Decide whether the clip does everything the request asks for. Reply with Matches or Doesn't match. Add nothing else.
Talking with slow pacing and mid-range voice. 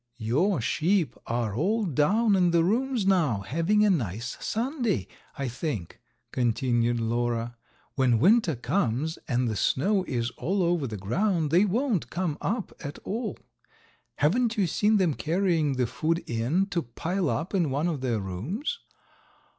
Doesn't match